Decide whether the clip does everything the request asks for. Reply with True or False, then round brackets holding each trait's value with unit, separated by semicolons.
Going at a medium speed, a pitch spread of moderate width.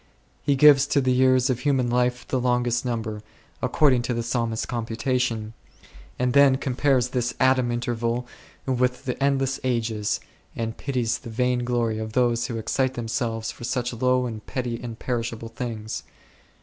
False (160 wpm; 1.8 semitones)